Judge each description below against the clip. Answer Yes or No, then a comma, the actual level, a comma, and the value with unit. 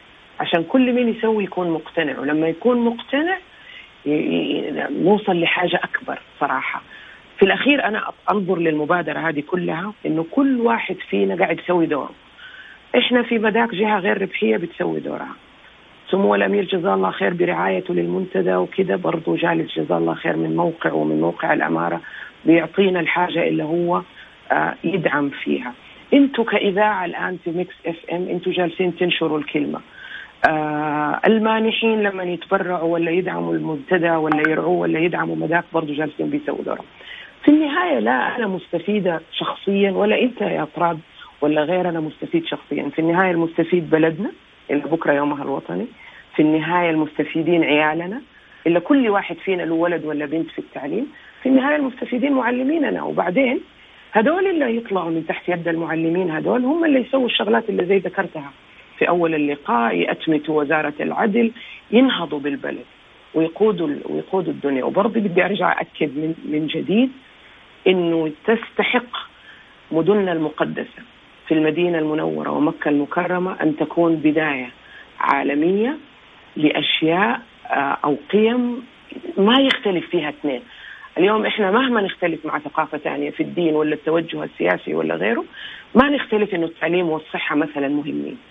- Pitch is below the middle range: No, medium, 175 Hz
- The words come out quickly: Yes, fast, 140 wpm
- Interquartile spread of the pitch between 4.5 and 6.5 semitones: Yes, wide, 5.6 semitones